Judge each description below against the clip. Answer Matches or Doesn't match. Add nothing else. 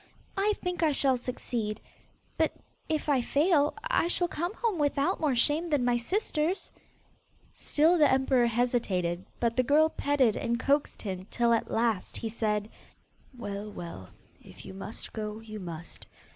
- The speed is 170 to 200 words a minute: Doesn't match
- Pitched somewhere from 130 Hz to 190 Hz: Doesn't match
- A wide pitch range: Matches